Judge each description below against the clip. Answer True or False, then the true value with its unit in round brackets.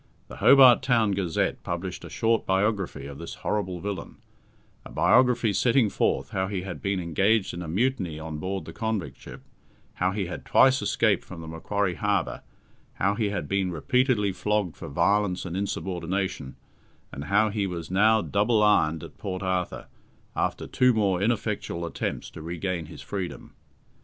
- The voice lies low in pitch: True (95 Hz)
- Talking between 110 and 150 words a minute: False (165 wpm)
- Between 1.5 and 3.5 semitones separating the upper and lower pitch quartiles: True (3.2 semitones)